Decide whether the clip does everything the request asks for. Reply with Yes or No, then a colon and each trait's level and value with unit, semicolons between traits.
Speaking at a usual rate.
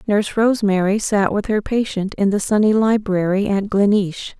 Yes: average, 165 wpm